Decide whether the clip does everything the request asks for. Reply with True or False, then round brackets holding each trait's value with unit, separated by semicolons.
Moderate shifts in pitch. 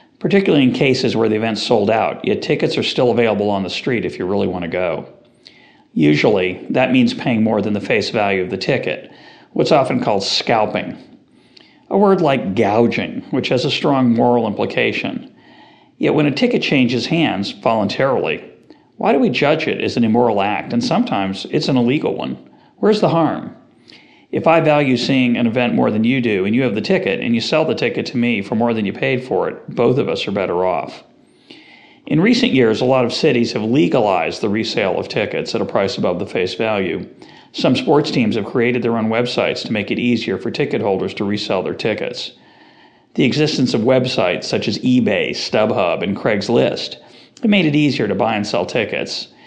False (5.7 semitones)